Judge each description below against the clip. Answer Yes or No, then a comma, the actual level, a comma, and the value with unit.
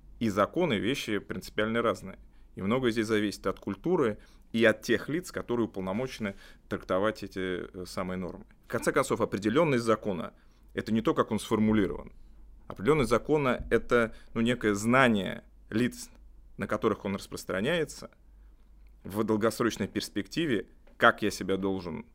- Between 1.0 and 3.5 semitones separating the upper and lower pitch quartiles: Yes, average, 3.2 semitones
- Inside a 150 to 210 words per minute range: No, average, 135 wpm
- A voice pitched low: Yes, low, 105 Hz